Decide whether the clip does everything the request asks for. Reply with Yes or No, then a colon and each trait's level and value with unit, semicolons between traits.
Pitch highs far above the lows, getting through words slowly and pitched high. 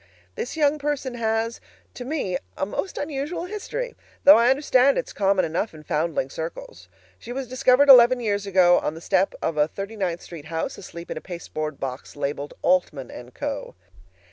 No: wide, 8.4 semitones; average, 185 wpm; high, 205 Hz